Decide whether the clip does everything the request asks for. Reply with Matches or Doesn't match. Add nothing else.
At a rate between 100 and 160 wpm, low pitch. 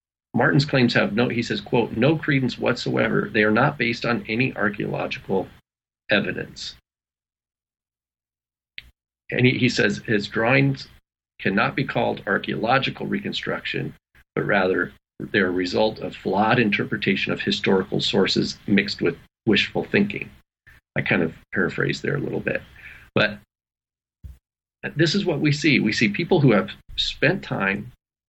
Matches